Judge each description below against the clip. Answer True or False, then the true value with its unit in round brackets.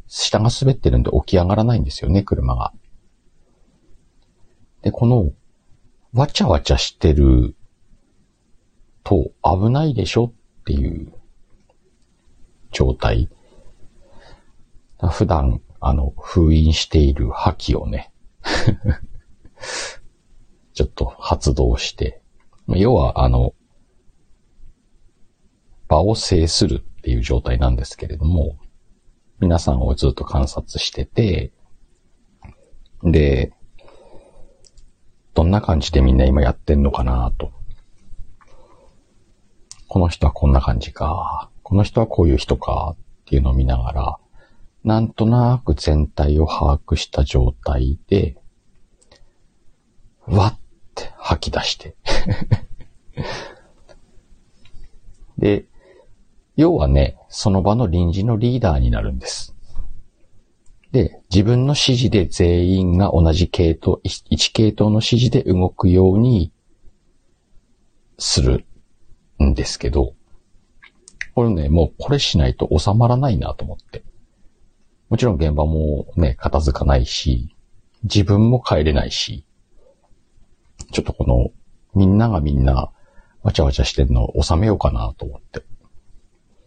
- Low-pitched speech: True (90 Hz)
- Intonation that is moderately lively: False (6.8 semitones)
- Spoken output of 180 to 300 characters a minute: True (215 characters per minute)